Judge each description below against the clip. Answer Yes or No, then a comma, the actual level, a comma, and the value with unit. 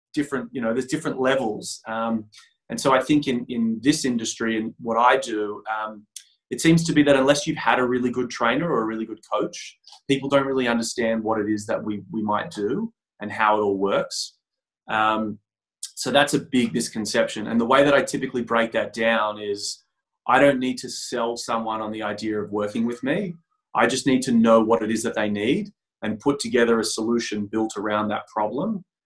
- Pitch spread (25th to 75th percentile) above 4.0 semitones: No, average, 3.5 semitones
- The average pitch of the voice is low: Yes, low, 115 Hz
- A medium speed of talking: No, fast, 215 wpm